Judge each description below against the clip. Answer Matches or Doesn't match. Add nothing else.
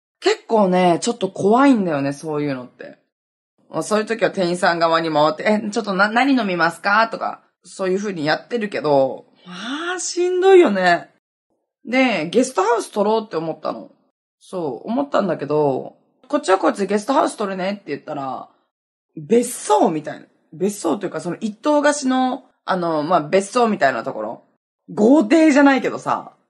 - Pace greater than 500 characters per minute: Doesn't match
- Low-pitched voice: Doesn't match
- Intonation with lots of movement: Matches